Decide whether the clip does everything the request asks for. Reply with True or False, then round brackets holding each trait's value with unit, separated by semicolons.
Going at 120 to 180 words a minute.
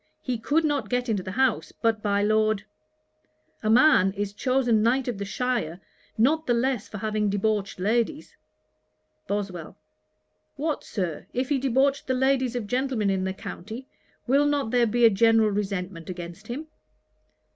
True (160 wpm)